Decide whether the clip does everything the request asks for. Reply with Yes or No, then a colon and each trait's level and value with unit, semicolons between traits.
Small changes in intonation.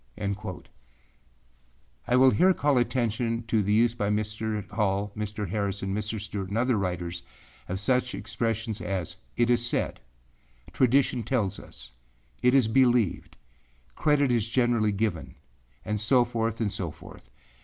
No: average, 3.7 semitones